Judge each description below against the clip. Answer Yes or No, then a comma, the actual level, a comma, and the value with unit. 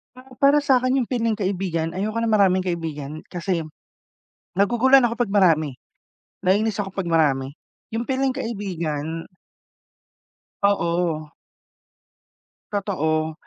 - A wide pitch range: Yes, wide, 5.8 semitones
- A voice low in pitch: No, high, 195 Hz